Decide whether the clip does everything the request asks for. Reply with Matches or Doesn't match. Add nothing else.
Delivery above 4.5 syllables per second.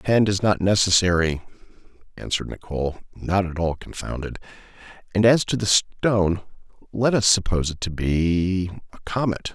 Matches